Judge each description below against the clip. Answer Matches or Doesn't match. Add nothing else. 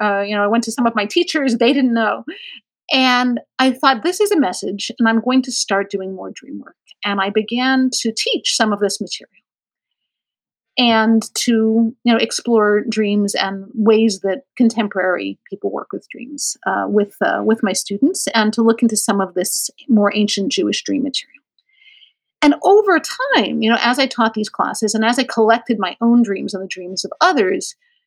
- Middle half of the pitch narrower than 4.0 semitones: Doesn't match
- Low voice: Doesn't match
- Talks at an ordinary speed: Matches